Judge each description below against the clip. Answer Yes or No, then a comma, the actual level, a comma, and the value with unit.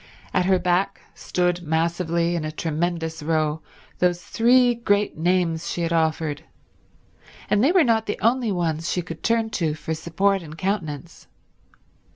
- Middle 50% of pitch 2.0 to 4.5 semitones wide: Yes, average, 3.7 semitones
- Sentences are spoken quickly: No, average, 155 wpm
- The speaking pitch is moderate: Yes, medium, 175 Hz